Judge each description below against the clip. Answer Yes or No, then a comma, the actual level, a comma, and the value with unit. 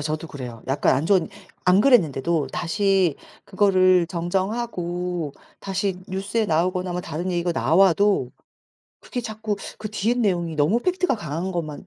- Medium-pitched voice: Yes, medium, 180 Hz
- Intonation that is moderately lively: Yes, average, 3.6 semitones